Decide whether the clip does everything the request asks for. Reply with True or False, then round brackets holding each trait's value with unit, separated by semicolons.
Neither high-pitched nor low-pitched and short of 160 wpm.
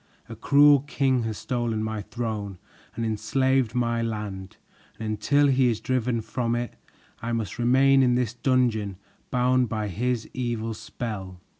False (120 Hz; 150 wpm)